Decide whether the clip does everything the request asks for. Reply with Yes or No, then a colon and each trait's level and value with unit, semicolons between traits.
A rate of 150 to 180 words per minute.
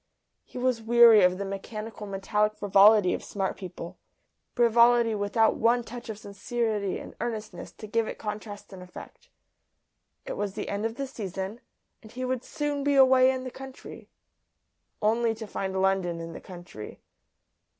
Yes: average, 160 wpm